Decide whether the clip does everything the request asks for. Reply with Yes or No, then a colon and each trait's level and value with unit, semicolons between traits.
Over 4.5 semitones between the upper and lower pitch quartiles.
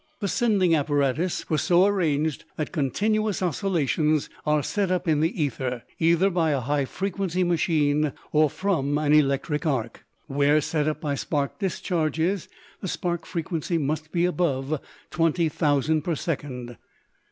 No: average, 3.6 semitones